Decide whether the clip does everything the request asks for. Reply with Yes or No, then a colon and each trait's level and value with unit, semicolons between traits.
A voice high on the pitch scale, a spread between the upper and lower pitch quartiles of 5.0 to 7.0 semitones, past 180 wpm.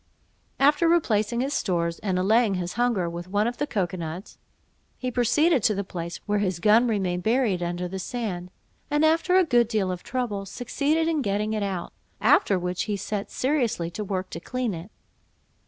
Yes: high, 210 Hz; average, 5.3 semitones; average, 190 wpm